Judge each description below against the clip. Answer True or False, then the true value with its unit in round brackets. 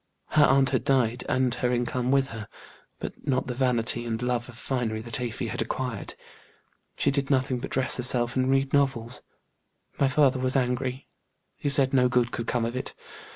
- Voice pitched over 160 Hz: False (125 Hz)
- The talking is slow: False (190 wpm)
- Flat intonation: True (1.8 semitones)